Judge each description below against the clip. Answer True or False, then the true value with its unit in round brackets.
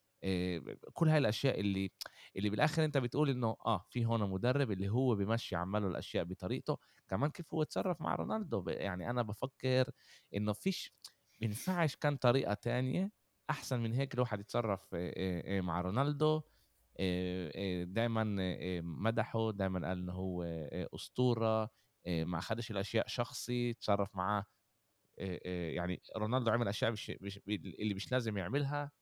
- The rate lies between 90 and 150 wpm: True (130 wpm)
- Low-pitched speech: True (110 Hz)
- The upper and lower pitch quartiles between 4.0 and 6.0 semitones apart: True (4.7 semitones)